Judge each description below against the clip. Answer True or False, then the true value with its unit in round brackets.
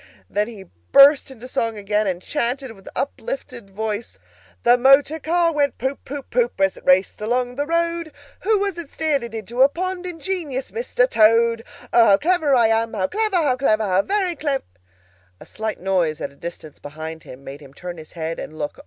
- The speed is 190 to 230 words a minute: True (195 wpm)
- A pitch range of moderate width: False (7.7 semitones)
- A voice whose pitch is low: False (240 Hz)